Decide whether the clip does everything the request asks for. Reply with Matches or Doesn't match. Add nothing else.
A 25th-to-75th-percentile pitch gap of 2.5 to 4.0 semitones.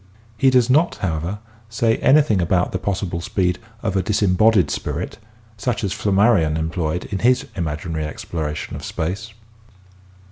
Doesn't match